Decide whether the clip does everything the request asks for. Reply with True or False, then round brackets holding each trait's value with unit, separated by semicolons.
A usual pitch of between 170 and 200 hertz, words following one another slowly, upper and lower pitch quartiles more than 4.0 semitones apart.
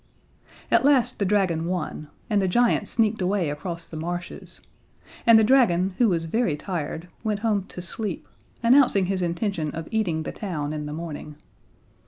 False (185 Hz; 170 wpm; 4.7 semitones)